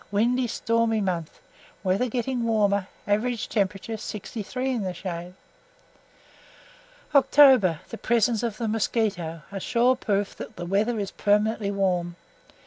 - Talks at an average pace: No, slow, 130 wpm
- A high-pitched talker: Yes, high, 210 Hz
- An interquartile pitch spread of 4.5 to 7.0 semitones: No, average, 3.4 semitones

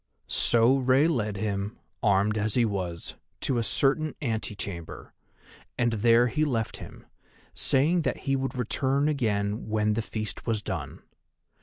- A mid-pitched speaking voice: No, low, 115 Hz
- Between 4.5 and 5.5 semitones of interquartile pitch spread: No, average, 4.1 semitones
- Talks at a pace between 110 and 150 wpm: Yes, average, 145 wpm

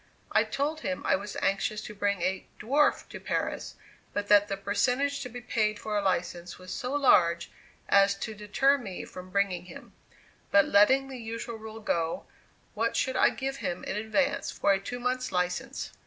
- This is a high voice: Yes, high, 210 Hz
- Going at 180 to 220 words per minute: Yes, average, 185 wpm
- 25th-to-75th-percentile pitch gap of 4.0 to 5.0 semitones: Yes, average, 4.4 semitones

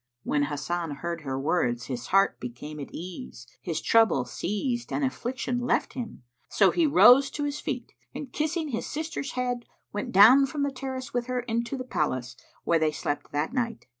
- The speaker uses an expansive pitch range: Yes, wide, 9.0 semitones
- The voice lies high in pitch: Yes, high, 230 Hz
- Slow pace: No, average, 185 wpm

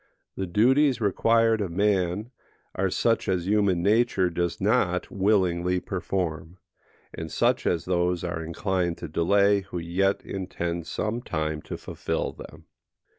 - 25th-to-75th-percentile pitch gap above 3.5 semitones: No, average, 3.0 semitones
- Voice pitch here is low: Yes, very low, 95 Hz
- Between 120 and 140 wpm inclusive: Yes, slow, 135 wpm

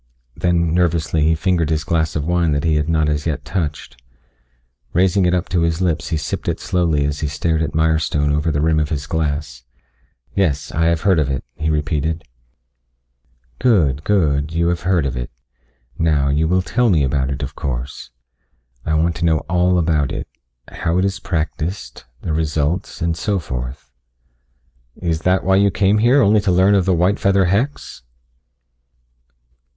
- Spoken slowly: No, average, 180 wpm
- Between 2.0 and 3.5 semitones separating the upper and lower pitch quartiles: Yes, average, 3.2 semitones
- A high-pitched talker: No, very low, 80 Hz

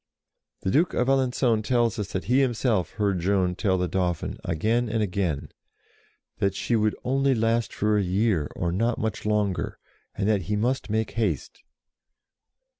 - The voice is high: No, low, 105 Hz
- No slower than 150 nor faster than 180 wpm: Yes, average, 165 wpm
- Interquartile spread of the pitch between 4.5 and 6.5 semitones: No, average, 3.7 semitones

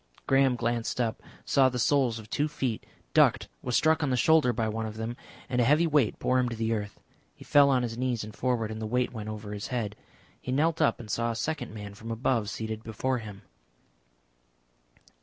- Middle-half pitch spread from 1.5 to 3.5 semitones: Yes, average, 3.0 semitones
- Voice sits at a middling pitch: No, low, 120 Hz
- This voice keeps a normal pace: No, fast, 215 wpm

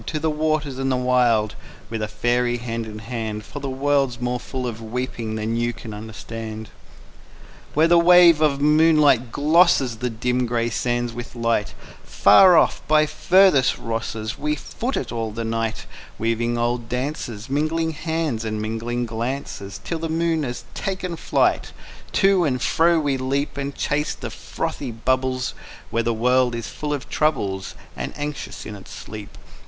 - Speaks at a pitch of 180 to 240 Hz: No, low, 125 Hz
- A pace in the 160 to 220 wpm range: Yes, average, 170 wpm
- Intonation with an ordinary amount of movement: Yes, average, 4.8 semitones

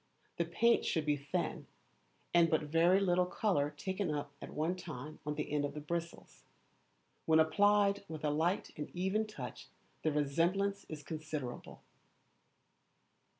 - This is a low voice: No, medium, 160 Hz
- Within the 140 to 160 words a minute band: Yes, average, 150 wpm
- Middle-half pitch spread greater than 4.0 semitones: No, average, 3.7 semitones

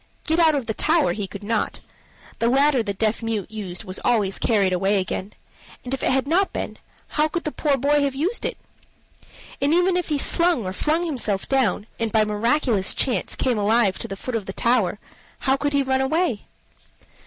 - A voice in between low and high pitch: No, high, 245 Hz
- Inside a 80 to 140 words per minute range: No, fast, 205 wpm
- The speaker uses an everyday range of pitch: No, wide, 6.0 semitones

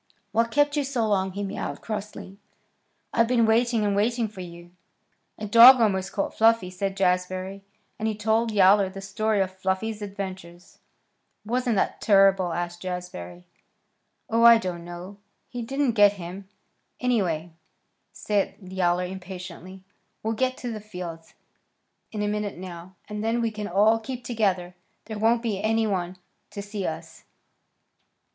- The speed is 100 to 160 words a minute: Yes, average, 150 wpm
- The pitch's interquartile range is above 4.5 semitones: No, average, 3.3 semitones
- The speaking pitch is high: Yes, high, 200 Hz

